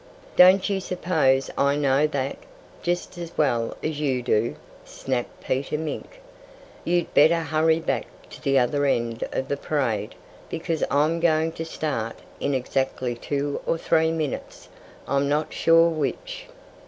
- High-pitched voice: No, medium, 150 Hz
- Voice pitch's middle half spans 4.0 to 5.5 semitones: No, average, 3.5 semitones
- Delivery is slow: No, average, 145 wpm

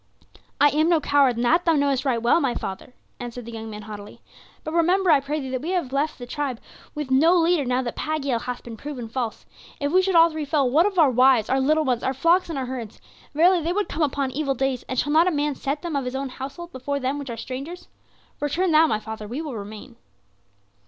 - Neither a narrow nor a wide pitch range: Yes, average, 3.9 semitones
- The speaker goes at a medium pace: No, fast, 245 wpm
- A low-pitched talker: No, very high, 275 Hz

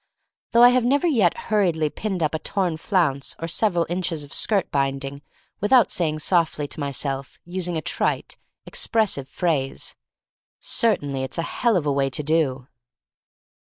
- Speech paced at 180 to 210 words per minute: No, average, 160 wpm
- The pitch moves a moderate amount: No, wide, 5.7 semitones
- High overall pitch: No, medium, 165 Hz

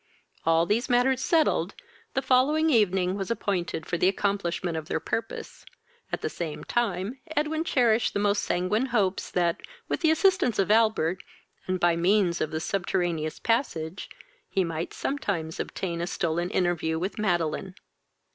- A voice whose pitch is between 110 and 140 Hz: No, high, 190 Hz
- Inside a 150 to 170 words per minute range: Yes, average, 155 wpm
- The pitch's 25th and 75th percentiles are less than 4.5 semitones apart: No, average, 5.2 semitones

